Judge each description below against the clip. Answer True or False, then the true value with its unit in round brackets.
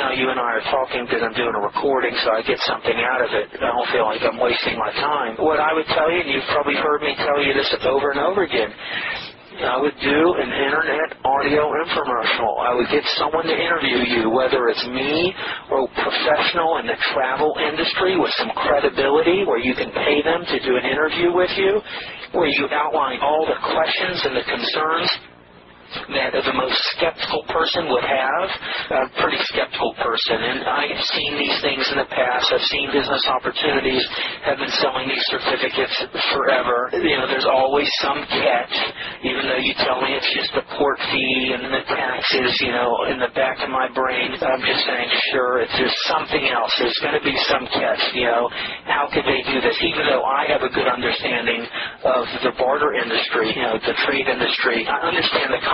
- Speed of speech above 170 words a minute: True (200 wpm)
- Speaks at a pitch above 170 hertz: False (140 Hz)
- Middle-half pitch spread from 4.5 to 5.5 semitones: False (3.3 semitones)